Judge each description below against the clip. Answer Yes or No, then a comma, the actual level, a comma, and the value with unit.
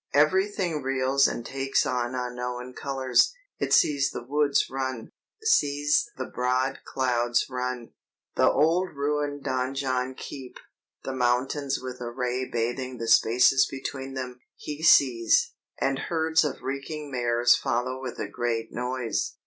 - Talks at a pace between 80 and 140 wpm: Yes, slow, 135 wpm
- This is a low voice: Yes, low, 130 Hz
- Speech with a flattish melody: Yes, narrow, 2.2 semitones